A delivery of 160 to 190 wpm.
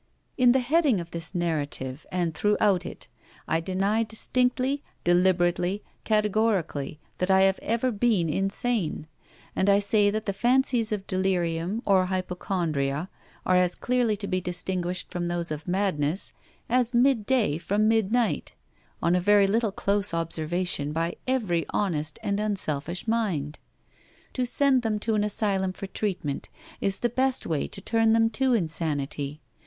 No: average, 150 wpm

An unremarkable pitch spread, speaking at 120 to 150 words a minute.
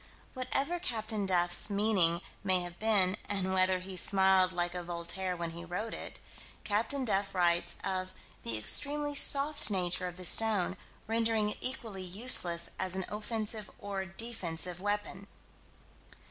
Yes: average, 3.4 semitones; average, 145 wpm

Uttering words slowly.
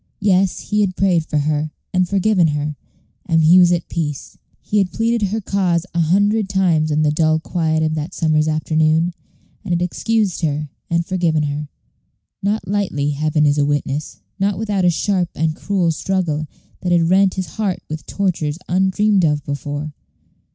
No: average, 175 wpm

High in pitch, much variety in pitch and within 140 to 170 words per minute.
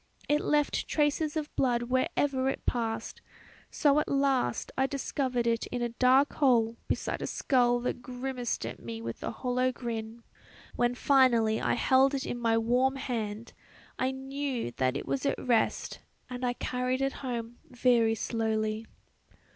No: high, 245 Hz; average, 2.7 semitones; average, 160 wpm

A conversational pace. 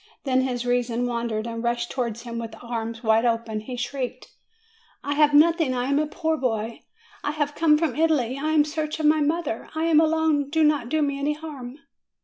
No: fast, 210 wpm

